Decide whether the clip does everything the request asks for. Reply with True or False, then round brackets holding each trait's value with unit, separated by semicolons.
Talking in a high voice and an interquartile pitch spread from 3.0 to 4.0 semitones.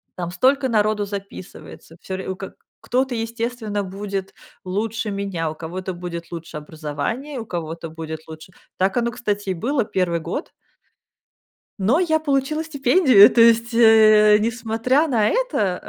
False (210 Hz; 4.9 semitones)